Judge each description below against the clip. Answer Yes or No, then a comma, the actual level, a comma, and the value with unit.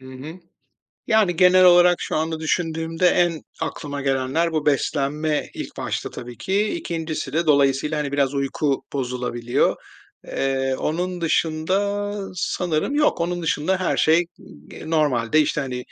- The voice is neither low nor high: Yes, medium, 155 Hz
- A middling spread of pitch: Yes, average, 4.1 semitones